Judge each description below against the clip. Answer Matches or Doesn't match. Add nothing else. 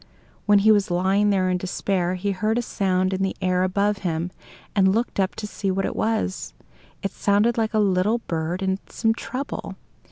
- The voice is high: Matches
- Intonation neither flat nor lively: Doesn't match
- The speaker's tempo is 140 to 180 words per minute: Doesn't match